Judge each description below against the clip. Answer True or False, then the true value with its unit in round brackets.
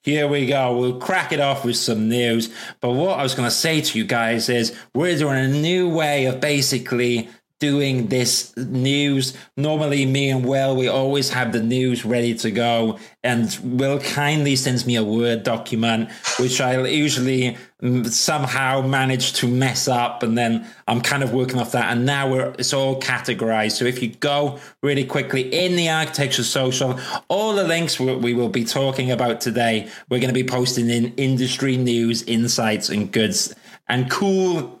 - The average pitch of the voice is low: True (130 Hz)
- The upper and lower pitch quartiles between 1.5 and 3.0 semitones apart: True (2.5 semitones)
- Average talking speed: True (180 wpm)